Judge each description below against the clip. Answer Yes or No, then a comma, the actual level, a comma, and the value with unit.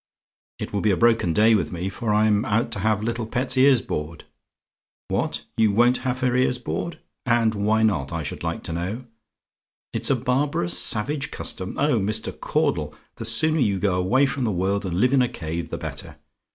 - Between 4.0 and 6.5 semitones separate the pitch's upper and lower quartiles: Yes, average, 4.6 semitones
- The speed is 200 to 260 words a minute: Yes, fast, 205 wpm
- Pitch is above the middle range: No, low, 110 Hz